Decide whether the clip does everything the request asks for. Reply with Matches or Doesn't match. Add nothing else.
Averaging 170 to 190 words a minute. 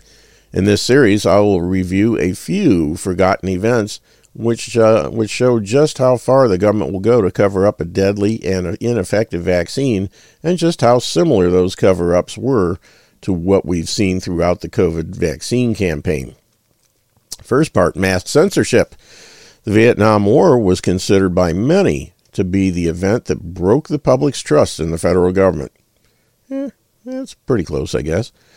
Doesn't match